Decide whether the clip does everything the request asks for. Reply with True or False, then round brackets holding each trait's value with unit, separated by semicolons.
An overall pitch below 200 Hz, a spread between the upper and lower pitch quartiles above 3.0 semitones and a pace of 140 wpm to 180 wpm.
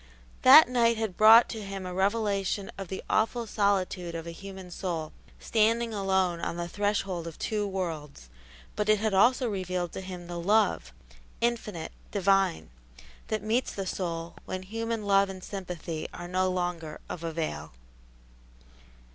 True (190 Hz; 3.5 semitones; 155 wpm)